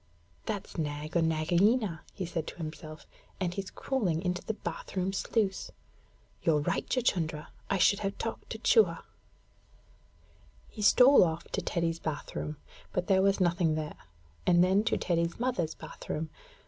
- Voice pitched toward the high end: No, medium, 175 Hz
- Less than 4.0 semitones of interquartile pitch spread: Yes, average, 3.5 semitones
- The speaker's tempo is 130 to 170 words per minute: Yes, average, 160 wpm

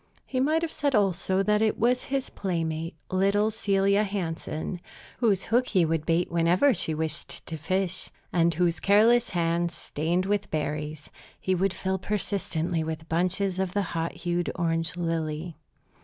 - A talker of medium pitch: Yes, medium, 180 Hz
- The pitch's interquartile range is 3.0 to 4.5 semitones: Yes, average, 3.5 semitones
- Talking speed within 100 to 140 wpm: No, average, 155 wpm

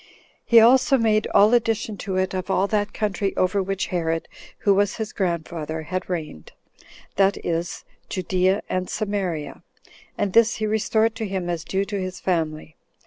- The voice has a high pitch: Yes, high, 195 Hz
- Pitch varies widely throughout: No, average, 3.3 semitones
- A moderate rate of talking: Yes, average, 165 wpm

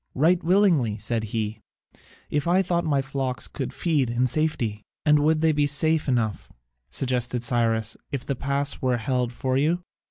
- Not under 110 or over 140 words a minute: No, average, 170 wpm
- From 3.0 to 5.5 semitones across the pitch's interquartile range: Yes, average, 4.5 semitones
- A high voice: No, low, 135 Hz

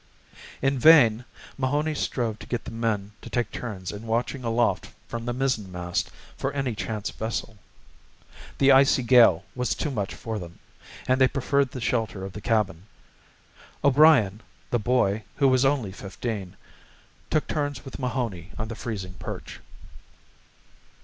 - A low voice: Yes, low, 115 Hz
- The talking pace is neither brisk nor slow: Yes, average, 150 wpm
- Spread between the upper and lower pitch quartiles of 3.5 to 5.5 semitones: Yes, average, 4.0 semitones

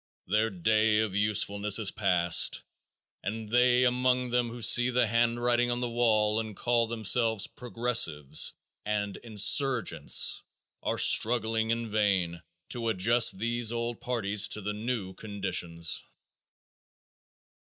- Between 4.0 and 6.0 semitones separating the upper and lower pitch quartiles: No, narrow, 2.6 semitones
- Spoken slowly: Yes, slow, 120 wpm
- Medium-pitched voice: No, low, 110 Hz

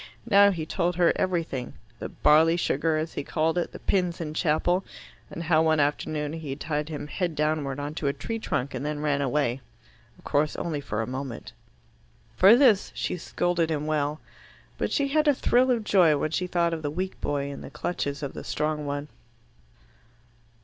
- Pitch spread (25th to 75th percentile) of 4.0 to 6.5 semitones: No, average, 3.3 semitones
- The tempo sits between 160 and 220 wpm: Yes, average, 200 wpm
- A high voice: No, medium, 155 Hz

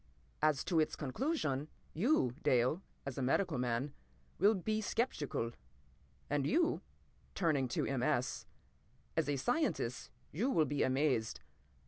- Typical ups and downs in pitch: No, wide, 7.2 semitones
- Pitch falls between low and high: Yes, medium, 145 Hz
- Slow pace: Yes, slow, 120 wpm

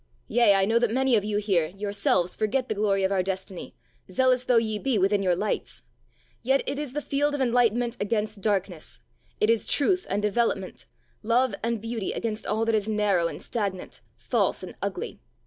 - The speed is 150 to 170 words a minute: No, average, 190 wpm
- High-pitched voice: Yes, high, 215 Hz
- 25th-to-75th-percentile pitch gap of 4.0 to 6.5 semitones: No, average, 3.3 semitones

